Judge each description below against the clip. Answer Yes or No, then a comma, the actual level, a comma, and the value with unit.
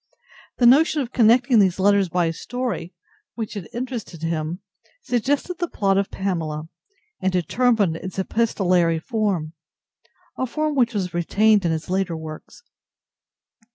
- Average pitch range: No, wide, 6.0 semitones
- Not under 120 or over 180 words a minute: Yes, slow, 135 wpm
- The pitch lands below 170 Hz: No, high, 195 Hz